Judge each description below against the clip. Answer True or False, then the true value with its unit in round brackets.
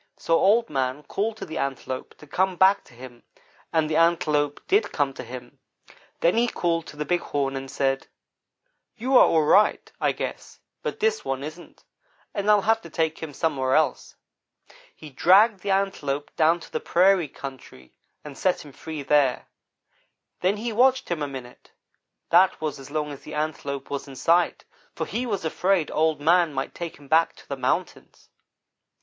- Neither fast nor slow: True (185 wpm)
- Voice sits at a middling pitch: True (155 Hz)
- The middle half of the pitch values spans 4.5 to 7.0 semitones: True (5.2 semitones)